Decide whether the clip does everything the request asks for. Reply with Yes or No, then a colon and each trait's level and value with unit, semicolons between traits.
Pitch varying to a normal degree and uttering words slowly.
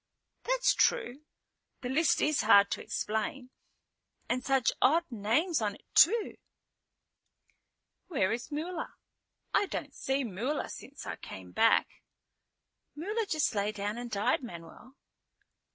No: wide, 6.6 semitones; slow, 125 wpm